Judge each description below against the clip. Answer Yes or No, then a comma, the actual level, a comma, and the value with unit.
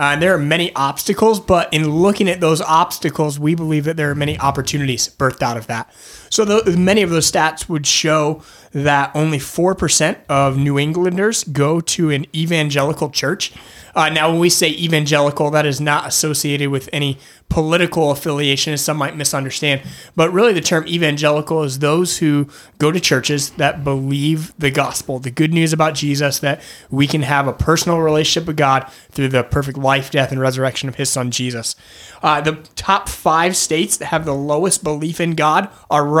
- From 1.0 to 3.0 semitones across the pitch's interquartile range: Yes, narrow, 2.5 semitones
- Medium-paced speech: Yes, average, 190 wpm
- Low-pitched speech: No, medium, 150 Hz